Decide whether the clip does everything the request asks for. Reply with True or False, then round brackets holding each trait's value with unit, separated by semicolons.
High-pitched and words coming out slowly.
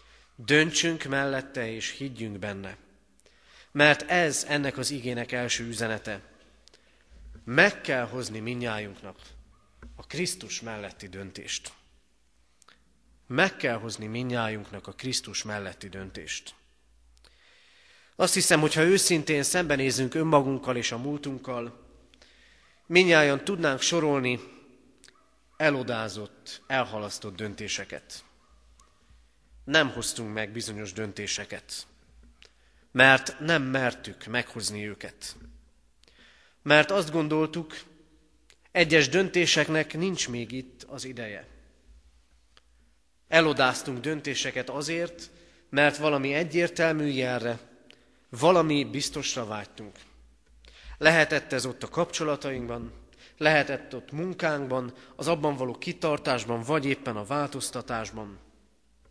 False (125 Hz; 90 wpm)